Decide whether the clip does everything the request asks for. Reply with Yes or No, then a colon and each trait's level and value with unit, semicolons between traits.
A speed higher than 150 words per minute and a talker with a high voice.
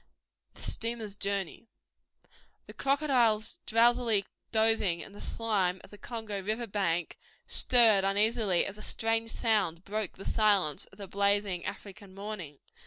No: slow, 135 wpm; high, 210 Hz